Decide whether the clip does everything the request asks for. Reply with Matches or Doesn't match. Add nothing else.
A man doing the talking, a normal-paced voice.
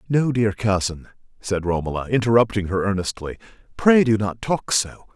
Matches